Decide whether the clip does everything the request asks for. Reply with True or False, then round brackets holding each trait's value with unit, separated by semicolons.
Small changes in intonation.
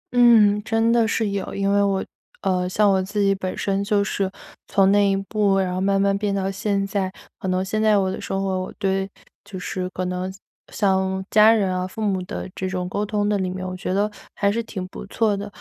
True (1.6 semitones)